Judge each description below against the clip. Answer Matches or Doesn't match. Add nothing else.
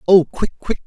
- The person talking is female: Doesn't match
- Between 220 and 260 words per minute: Doesn't match